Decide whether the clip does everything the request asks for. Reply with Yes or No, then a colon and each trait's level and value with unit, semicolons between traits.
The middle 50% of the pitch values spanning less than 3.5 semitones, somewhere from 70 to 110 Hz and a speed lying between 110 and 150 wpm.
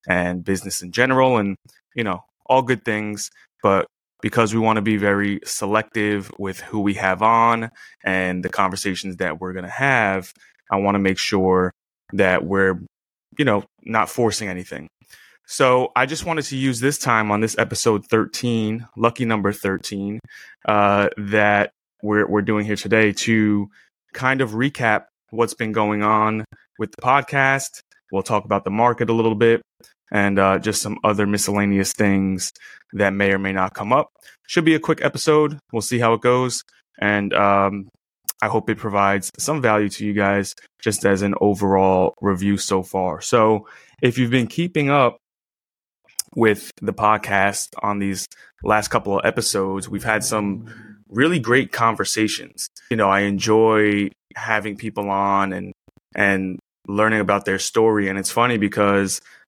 No: narrow, 2.5 semitones; low, 105 Hz; average, 165 wpm